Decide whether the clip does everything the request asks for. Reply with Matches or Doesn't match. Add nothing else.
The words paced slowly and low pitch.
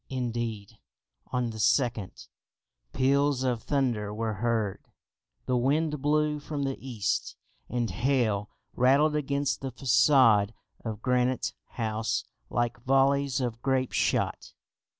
Matches